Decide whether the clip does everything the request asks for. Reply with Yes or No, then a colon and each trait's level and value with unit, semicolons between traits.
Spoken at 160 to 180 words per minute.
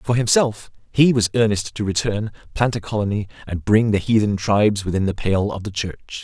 No: average, 200 wpm